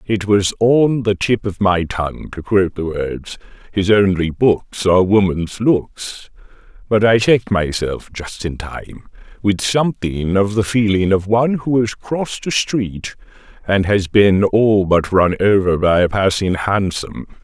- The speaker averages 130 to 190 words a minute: Yes, average, 160 wpm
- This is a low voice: Yes, low, 100 Hz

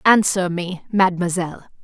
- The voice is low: No, medium, 185 Hz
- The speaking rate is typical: No, slow, 100 wpm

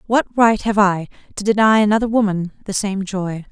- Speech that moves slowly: No, average, 190 wpm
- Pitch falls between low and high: No, high, 205 Hz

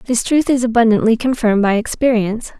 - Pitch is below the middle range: No, high, 230 Hz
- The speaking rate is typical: Yes, average, 160 wpm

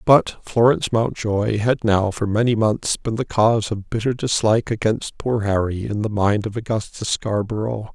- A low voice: Yes, low, 110 Hz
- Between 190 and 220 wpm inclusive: No, average, 175 wpm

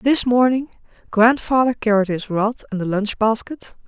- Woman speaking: Yes, female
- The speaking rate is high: No, average, 155 wpm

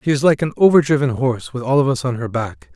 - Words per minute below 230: No, fast, 285 wpm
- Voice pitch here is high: No, low, 130 Hz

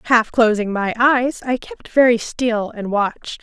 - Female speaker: Yes, female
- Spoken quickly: No, average, 175 wpm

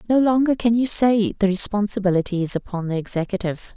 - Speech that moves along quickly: No, average, 175 wpm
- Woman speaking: Yes, female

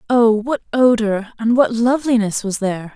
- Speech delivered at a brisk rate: No, average, 160 wpm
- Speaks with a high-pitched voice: Yes, high, 225 Hz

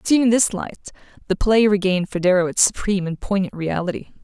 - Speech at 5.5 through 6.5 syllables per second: Yes, 6.3 syllables/s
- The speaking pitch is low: No, high, 195 Hz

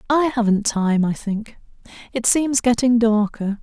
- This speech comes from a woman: Yes, female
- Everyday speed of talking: Yes, average, 150 wpm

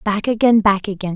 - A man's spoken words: No, female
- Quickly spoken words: Yes, fast, 210 wpm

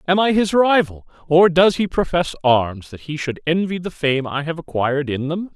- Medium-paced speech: No, fast, 215 wpm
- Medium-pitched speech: Yes, medium, 160 Hz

